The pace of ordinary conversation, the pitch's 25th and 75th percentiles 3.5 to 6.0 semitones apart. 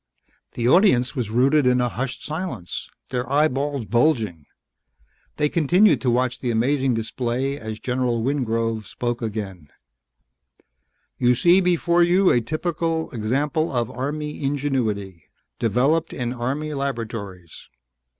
No: slow, 120 wpm; average, 4.5 semitones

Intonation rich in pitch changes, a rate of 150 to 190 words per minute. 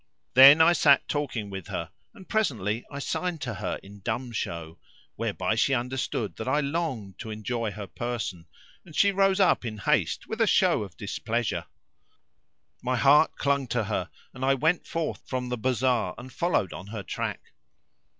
Yes: wide, 5.7 semitones; average, 175 wpm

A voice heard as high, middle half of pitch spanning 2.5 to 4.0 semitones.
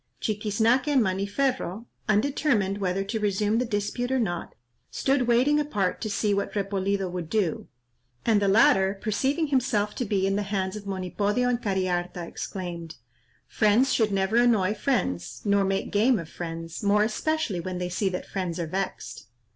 Yes: high, 205 Hz; average, 3.6 semitones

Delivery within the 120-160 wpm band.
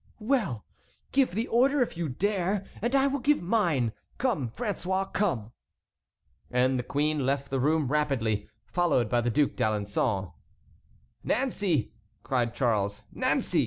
Yes: slow, 135 wpm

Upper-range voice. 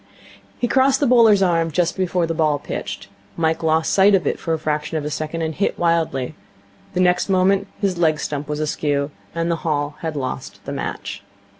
No: medium, 165 Hz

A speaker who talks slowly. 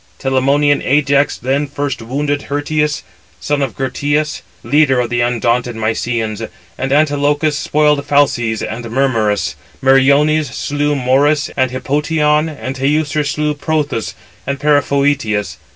Yes: slow, 120 wpm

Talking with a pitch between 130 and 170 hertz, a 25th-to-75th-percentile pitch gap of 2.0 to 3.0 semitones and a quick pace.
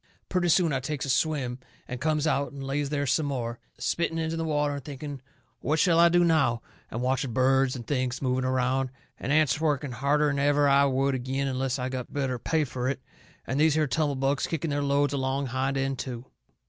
Yes: medium, 140 Hz; narrow, 2.4 semitones; fast, 210 wpm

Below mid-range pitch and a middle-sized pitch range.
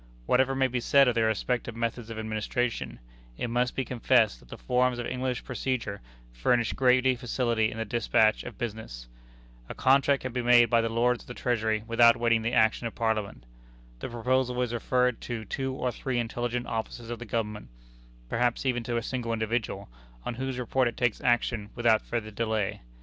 No: low, 120 Hz; narrow, 1.9 semitones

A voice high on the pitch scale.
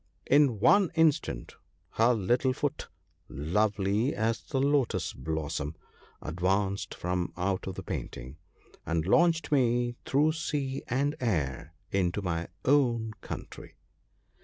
No: low, 110 Hz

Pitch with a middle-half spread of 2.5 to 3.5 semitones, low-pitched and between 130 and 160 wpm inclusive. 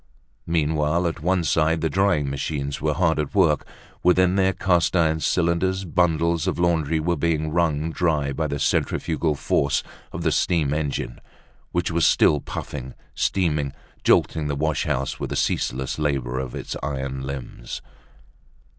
Yes: average, 2.9 semitones; very low, 80 Hz; average, 155 wpm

